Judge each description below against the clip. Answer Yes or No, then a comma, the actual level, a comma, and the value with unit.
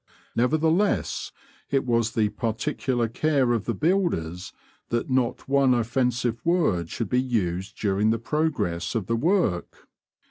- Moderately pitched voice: No, low, 120 Hz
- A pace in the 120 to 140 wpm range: Yes, slow, 135 wpm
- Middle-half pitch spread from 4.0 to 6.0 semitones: Yes, average, 4.4 semitones